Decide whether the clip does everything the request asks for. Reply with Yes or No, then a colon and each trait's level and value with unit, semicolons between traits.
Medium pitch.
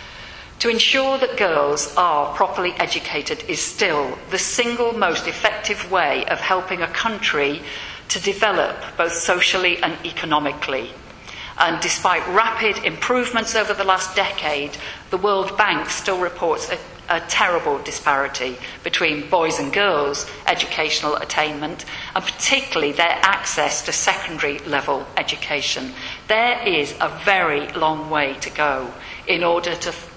Yes: medium, 180 Hz